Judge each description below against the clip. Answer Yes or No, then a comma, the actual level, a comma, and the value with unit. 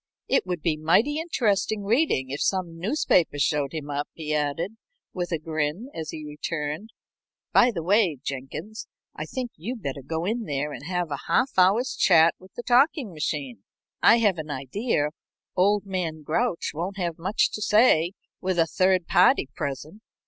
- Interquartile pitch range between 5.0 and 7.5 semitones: Yes, wide, 5.6 semitones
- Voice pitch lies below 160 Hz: No, medium, 175 Hz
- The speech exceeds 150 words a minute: Yes, average, 170 wpm